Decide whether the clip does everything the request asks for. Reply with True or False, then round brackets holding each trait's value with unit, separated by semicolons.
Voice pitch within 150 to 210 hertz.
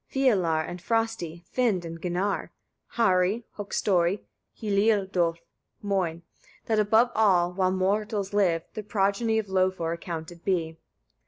True (190 Hz)